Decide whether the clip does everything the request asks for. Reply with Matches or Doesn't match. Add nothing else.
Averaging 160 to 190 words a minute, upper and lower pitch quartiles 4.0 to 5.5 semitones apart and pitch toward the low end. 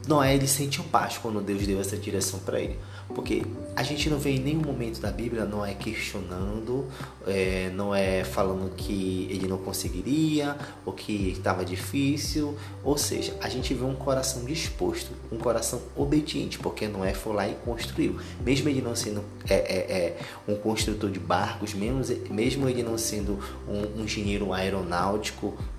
Matches